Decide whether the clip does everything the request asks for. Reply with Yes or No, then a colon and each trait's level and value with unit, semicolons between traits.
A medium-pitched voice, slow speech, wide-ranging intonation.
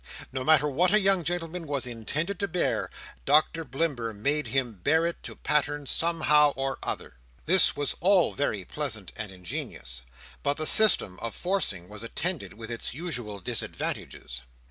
No: medium, 145 Hz; average, 155 wpm; wide, 6.7 semitones